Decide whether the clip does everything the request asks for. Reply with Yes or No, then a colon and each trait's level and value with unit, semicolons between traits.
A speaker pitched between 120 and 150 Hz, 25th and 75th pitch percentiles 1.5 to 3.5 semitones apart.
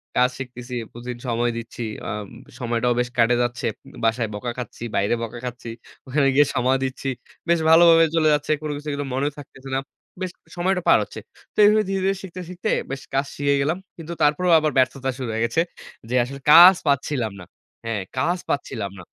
No: low, 135 Hz; average, 4.4 semitones